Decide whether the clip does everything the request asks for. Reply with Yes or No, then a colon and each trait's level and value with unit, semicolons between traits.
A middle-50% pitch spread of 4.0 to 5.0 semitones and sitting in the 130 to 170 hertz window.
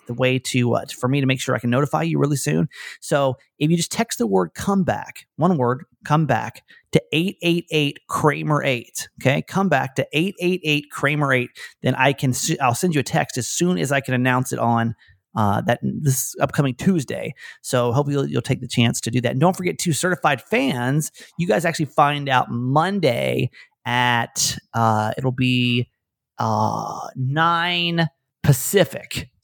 Yes: average, 4.7 semitones; medium, 140 Hz